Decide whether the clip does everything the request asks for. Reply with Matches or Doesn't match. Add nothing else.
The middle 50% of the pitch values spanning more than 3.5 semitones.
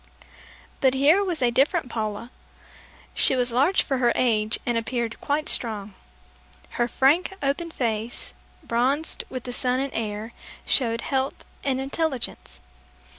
Doesn't match